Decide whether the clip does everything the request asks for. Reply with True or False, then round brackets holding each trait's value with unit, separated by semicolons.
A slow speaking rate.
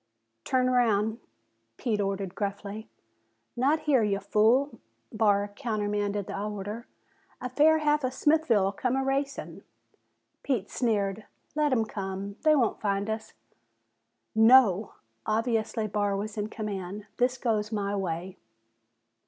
True (120 wpm)